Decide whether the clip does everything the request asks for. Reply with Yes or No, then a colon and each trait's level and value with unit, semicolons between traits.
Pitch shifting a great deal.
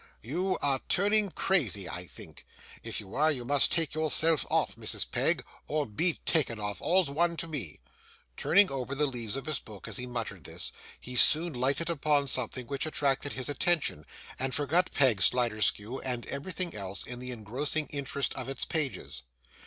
No: average, 4.5 semitones